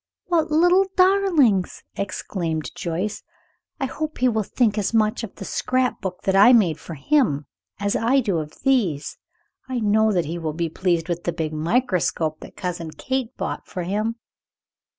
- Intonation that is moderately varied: No, wide, 7.0 semitones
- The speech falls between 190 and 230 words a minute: No, average, 170 wpm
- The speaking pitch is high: Yes, high, 205 Hz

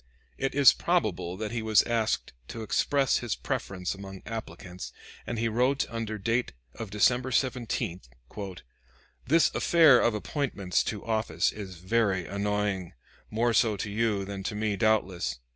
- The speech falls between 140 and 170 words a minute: Yes, average, 145 wpm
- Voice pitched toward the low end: Yes, low, 110 Hz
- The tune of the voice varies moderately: Yes, average, 3.3 semitones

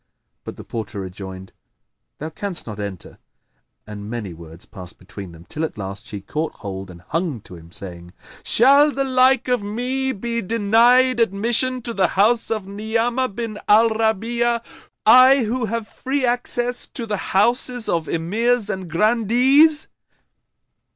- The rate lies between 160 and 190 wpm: No, average, 150 wpm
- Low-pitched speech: No, high, 215 Hz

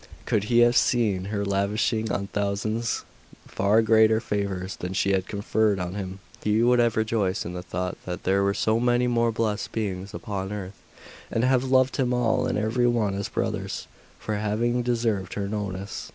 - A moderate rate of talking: Yes, average, 180 wpm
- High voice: No, low, 105 Hz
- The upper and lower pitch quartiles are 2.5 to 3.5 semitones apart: Yes, average, 2.8 semitones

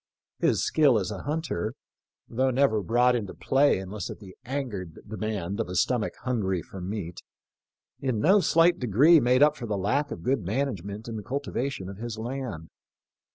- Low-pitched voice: Yes, low, 115 Hz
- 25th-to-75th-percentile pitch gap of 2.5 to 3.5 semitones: No, wide, 5.4 semitones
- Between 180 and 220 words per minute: Yes, average, 190 wpm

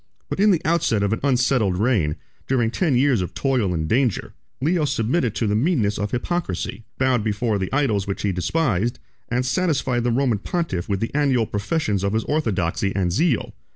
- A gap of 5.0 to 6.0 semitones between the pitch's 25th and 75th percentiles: Yes, wide, 5.5 semitones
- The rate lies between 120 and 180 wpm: No, average, 190 wpm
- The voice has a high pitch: No, low, 120 Hz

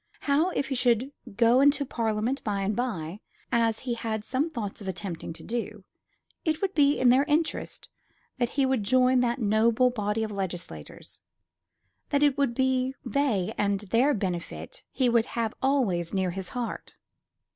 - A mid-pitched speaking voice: No, high, 235 Hz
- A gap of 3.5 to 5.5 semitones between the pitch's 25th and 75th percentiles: Yes, average, 4.4 semitones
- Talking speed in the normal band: Yes, average, 165 wpm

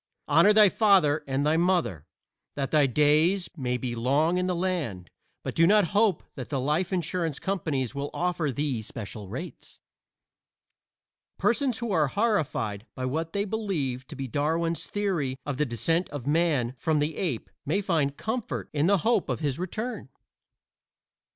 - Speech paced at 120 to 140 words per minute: No, average, 165 wpm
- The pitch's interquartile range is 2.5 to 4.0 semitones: No, wide, 5.5 semitones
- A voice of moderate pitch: Yes, medium, 155 Hz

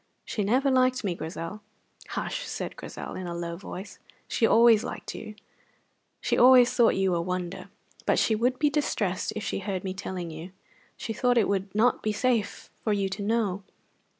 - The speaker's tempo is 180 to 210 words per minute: Yes, average, 185 wpm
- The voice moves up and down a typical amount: Yes, average, 4.2 semitones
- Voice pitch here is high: Yes, high, 205 Hz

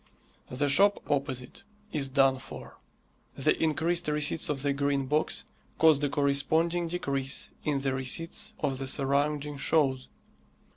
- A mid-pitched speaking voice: Yes, medium, 145 Hz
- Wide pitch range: No, narrow, 2.5 semitones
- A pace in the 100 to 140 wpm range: Yes, slow, 135 wpm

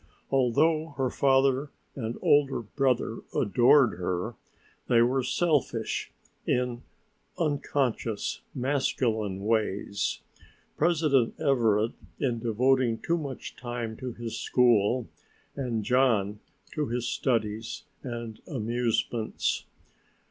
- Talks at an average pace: No, slow, 95 wpm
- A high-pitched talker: No, low, 120 Hz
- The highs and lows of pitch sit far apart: No, average, 3.3 semitones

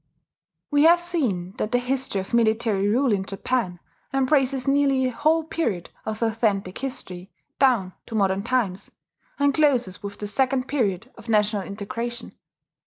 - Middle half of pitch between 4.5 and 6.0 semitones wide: Yes, average, 5.2 semitones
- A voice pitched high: Yes, high, 235 Hz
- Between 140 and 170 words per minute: Yes, average, 155 wpm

